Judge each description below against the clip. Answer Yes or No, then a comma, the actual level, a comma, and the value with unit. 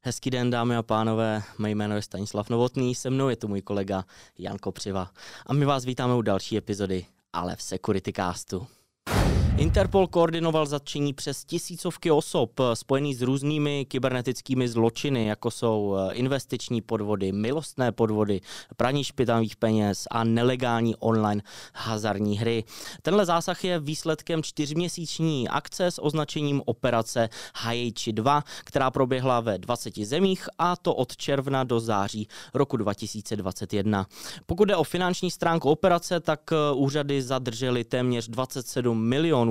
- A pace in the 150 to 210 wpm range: No, average, 135 wpm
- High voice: No, low, 125 Hz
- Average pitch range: Yes, average, 4.9 semitones